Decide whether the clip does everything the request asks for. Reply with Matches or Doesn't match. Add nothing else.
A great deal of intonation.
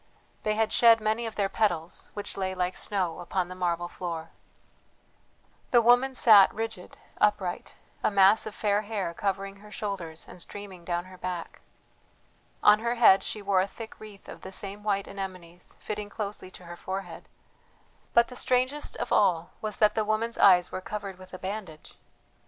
Doesn't match